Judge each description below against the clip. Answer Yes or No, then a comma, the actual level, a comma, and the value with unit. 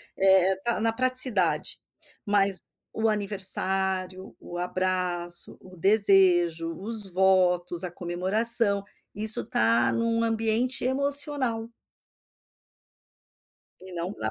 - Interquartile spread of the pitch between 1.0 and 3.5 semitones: No, average, 3.9 semitones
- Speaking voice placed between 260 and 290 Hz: No, high, 190 Hz